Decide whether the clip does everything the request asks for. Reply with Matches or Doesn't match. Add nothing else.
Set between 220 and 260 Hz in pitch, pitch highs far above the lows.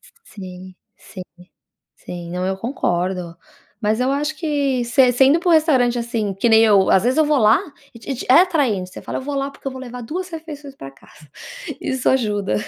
Matches